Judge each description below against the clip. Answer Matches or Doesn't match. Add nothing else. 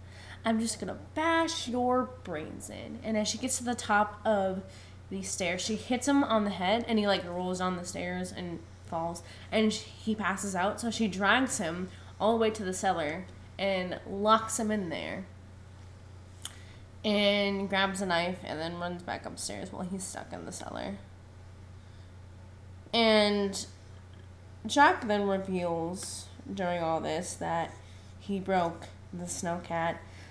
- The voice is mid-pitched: Matches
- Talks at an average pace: Matches